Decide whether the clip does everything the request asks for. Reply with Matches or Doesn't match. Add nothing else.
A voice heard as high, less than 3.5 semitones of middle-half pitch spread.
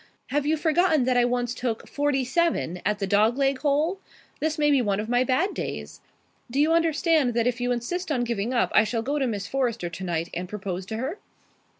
Doesn't match